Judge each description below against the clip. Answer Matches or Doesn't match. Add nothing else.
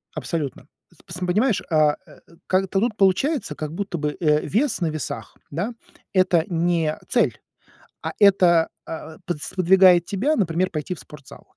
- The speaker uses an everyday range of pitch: Matches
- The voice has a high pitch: Doesn't match